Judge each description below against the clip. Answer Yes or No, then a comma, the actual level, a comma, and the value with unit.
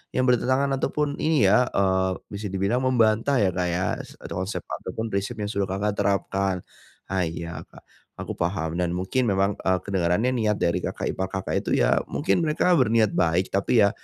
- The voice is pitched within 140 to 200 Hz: No, low, 100 Hz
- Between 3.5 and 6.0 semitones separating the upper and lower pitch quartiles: Yes, average, 4.1 semitones